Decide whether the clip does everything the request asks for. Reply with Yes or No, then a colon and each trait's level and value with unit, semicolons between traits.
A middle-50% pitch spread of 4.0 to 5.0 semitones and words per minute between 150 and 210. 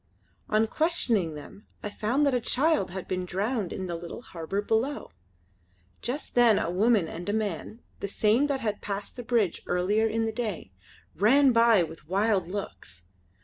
Yes: average, 4.4 semitones; average, 175 wpm